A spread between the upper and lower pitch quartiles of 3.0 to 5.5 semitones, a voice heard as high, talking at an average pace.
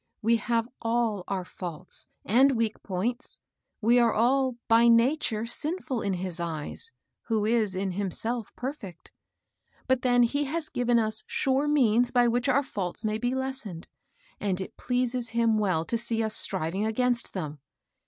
Yes: average, 3.6 semitones; high, 230 Hz; average, 165 wpm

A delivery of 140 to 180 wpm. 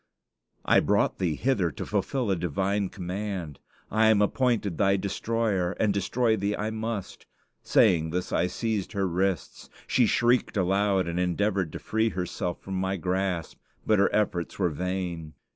Yes: average, 160 wpm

